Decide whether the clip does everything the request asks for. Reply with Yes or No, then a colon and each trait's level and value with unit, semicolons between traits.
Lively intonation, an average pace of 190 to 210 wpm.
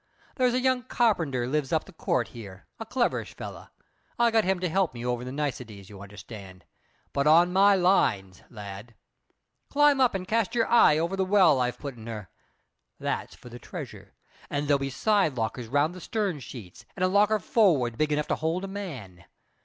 Yes: wide, 8.8 semitones; average, 195 wpm